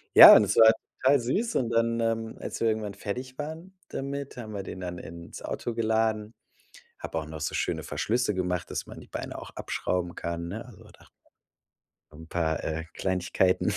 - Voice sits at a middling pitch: No, low, 110 Hz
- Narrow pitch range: No, average, 4.9 semitones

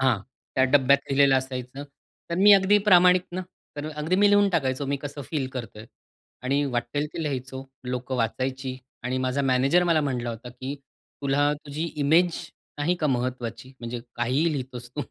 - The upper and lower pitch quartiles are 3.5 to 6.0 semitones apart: No, average, 3.0 semitones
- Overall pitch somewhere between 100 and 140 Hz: Yes, low, 135 Hz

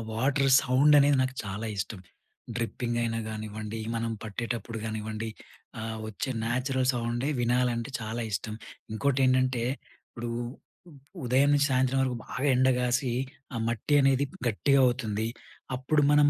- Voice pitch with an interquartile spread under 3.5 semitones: Yes, average, 2.8 semitones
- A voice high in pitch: No, low, 120 Hz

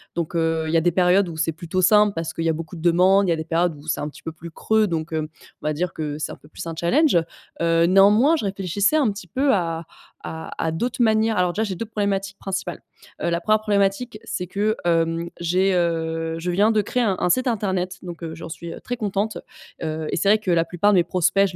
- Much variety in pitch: No, average, 3.7 semitones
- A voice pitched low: No, medium, 180 Hz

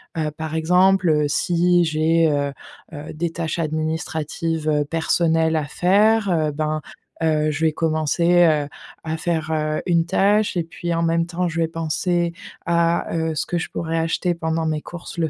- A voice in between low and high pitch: Yes, medium, 165 Hz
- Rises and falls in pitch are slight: Yes, narrow, 1.6 semitones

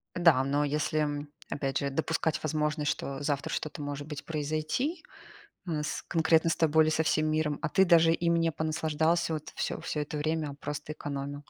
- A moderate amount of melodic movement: No, narrow, 1.7 semitones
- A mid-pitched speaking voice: Yes, medium, 155 Hz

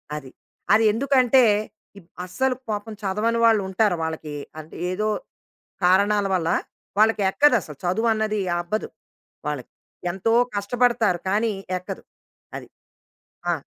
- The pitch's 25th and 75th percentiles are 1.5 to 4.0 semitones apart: Yes, average, 3.7 semitones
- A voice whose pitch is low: No, high, 210 Hz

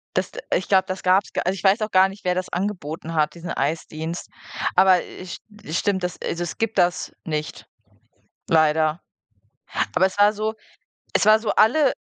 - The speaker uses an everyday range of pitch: Yes, average, 3.6 semitones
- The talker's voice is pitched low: No, medium, 185 Hz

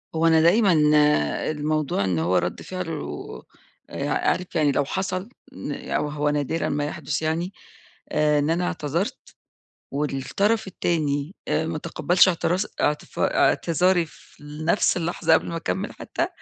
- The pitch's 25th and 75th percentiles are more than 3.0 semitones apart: Yes, average, 3.4 semitones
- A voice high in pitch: No, medium, 160 Hz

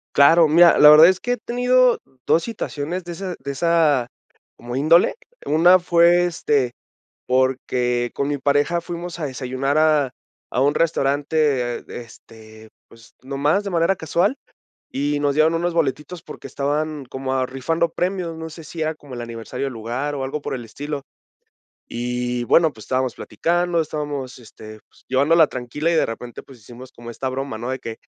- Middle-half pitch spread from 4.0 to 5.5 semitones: Yes, average, 4.4 semitones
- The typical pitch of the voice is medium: Yes, medium, 145 Hz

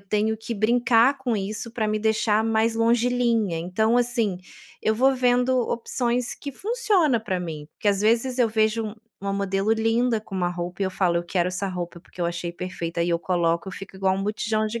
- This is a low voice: No, high, 215 Hz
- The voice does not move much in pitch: No, average, 4.0 semitones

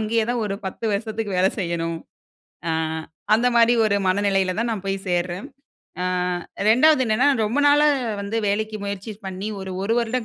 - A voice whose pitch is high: Yes, high, 215 Hz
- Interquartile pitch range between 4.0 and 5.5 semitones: No, average, 3.4 semitones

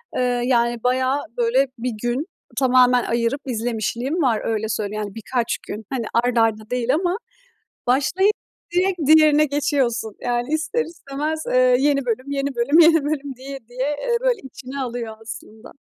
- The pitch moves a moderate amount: Yes, average, 3.4 semitones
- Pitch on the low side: No, very high, 255 Hz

